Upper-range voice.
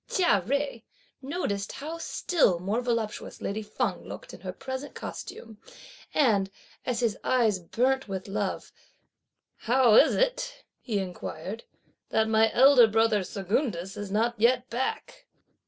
Yes: high, 225 Hz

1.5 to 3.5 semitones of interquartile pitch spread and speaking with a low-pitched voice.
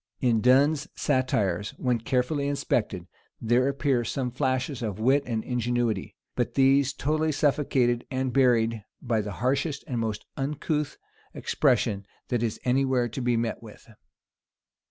Yes: average, 3.1 semitones; low, 125 Hz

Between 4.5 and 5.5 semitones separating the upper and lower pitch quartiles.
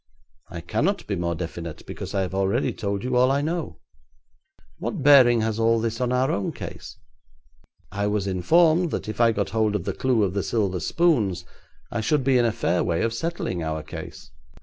Yes: average, 5.0 semitones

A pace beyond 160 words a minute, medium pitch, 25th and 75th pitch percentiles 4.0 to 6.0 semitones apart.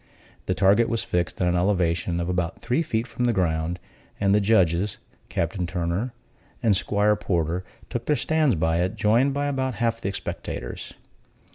No: average, 170 wpm; low, 100 Hz; average, 5.1 semitones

